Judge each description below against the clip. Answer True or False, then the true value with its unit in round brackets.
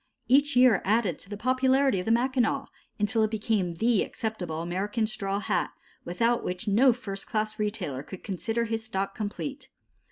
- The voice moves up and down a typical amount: True (3.4 semitones)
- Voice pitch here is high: True (215 Hz)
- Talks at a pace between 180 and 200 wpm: False (165 wpm)